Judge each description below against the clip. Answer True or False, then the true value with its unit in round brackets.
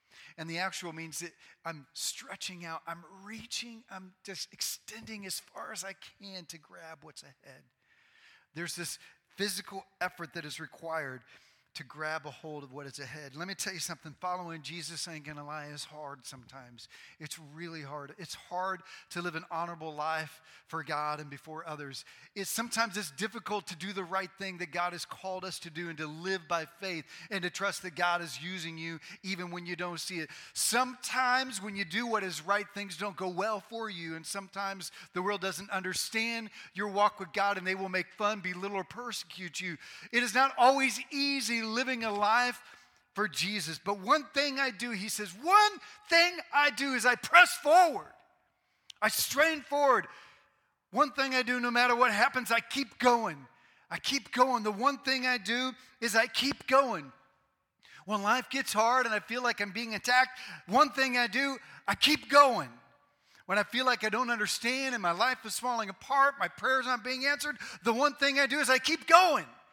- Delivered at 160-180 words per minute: False (195 wpm)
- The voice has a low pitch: False (200 Hz)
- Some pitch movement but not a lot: False (6.5 semitones)